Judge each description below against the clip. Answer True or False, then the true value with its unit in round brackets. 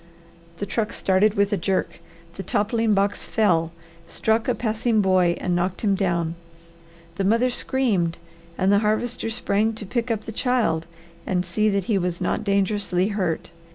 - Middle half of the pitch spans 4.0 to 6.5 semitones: False (3.1 semitones)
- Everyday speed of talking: True (165 wpm)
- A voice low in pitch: False (200 Hz)